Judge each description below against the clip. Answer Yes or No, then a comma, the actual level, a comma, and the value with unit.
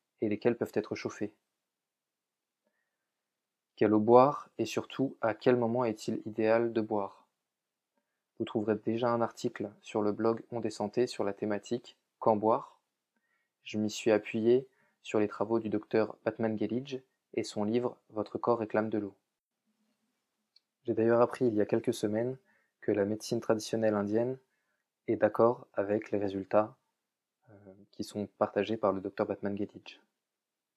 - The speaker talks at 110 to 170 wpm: Yes, average, 150 wpm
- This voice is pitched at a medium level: No, low, 110 Hz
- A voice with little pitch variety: Yes, narrow, 2.2 semitones